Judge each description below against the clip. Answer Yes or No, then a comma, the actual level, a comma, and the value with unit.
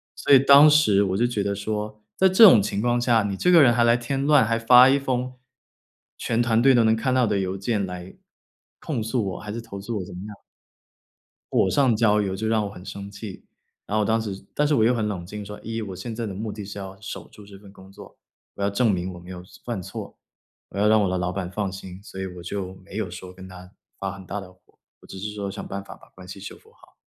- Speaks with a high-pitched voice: No, low, 105 Hz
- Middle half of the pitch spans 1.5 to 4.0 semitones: Yes, average, 3.5 semitones